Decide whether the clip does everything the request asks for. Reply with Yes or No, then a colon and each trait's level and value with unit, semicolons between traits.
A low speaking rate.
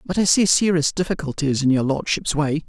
No: average, 200 wpm